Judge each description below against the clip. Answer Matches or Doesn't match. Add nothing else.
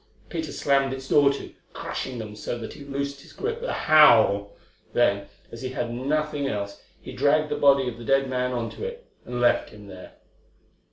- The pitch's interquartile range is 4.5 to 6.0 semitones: Doesn't match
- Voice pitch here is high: Doesn't match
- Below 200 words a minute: Doesn't match